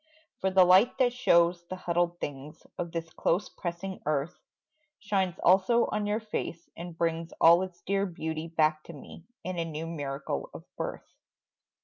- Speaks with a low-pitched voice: No, medium, 170 Hz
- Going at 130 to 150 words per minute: No, average, 165 wpm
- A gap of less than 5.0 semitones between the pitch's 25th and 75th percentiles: Yes, narrow, 2.6 semitones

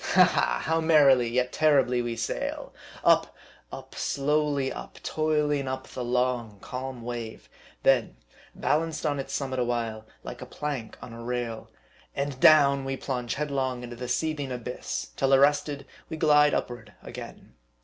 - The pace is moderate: Yes, average, 160 wpm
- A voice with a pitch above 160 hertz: No, low, 130 Hz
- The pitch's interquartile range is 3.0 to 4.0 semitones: Yes, average, 3.3 semitones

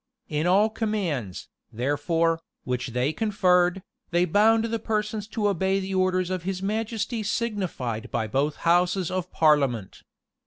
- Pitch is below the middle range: No, medium, 185 Hz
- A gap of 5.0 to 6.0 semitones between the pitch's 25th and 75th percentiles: Yes, wide, 5.6 semitones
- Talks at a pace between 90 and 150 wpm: Yes, average, 140 wpm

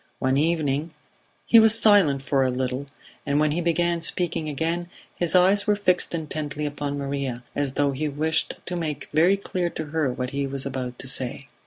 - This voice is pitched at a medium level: Yes, medium, 150 Hz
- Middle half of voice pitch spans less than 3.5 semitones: No, average, 3.8 semitones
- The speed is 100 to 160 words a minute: No, average, 190 wpm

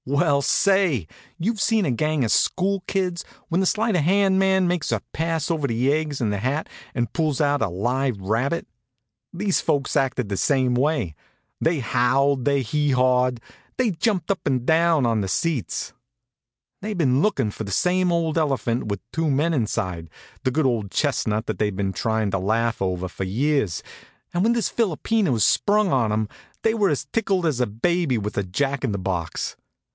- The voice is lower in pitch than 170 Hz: Yes, medium, 140 Hz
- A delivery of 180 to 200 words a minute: Yes, average, 190 wpm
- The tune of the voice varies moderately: No, wide, 7.1 semitones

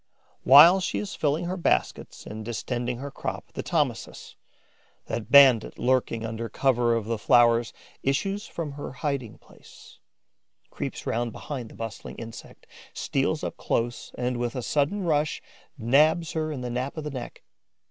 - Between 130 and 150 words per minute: No, average, 160 wpm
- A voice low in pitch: Yes, low, 125 Hz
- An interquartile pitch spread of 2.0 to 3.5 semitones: No, average, 4.1 semitones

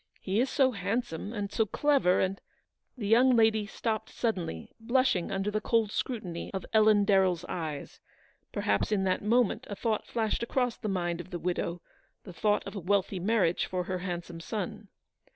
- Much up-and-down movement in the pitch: No, average, 3.8 semitones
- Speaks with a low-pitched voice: No, high, 205 Hz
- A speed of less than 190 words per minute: Yes, average, 180 wpm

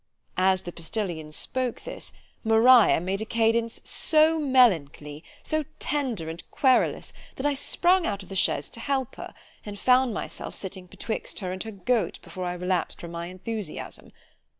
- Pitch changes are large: Yes, wide, 5.9 semitones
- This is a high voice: Yes, high, 215 Hz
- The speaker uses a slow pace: No, average, 165 wpm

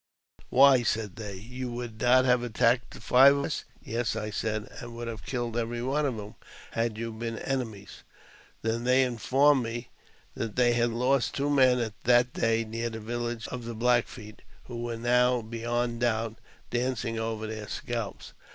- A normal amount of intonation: No, narrow, 1.7 semitones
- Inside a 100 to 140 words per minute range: No, average, 180 wpm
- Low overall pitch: Yes, low, 120 Hz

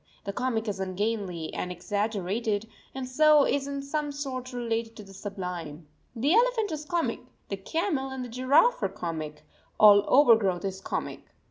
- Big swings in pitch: Yes, wide, 6.3 semitones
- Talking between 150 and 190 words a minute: Yes, average, 160 wpm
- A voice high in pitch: Yes, high, 230 Hz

